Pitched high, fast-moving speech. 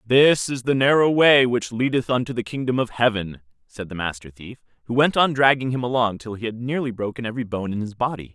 No: low, 120 Hz; fast, 230 wpm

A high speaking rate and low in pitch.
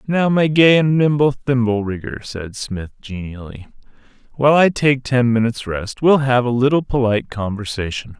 No: average, 160 wpm; low, 125 Hz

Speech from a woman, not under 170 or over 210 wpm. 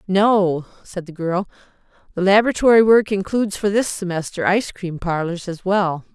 No: female; average, 155 wpm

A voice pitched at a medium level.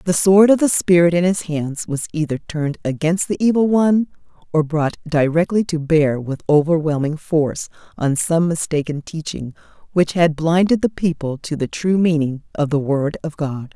Yes: medium, 160 Hz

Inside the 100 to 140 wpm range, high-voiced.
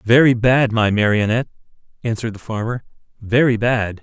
No: slow, 135 wpm; low, 115 Hz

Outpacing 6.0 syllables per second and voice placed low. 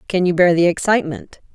No: 6.2 syllables/s; medium, 180 Hz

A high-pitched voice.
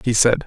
No: low, 115 Hz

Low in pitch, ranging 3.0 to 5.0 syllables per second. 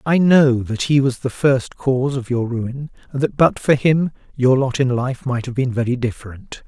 Yes: low, 130 Hz; 4.7 syllables/s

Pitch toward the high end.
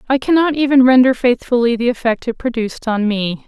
Yes: high, 245 Hz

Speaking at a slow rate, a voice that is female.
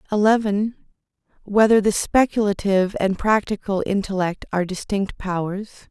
Yes: slow, 100 wpm; female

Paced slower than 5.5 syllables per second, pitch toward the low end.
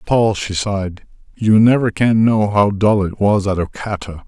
Yes: 4.5 syllables/s; low, 100 Hz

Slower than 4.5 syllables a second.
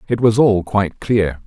No: 4.8 syllables/s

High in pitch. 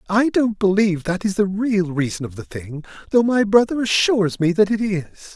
Yes: high, 195 Hz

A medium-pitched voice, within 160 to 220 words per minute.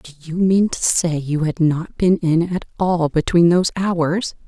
Yes: medium, 170 Hz; average, 200 wpm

